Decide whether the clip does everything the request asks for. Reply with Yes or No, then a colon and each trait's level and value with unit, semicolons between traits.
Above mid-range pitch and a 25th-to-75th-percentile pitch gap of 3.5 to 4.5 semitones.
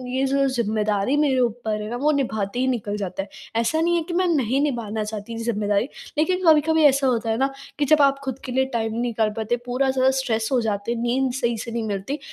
Yes: high, 240 Hz; average, 3.9 semitones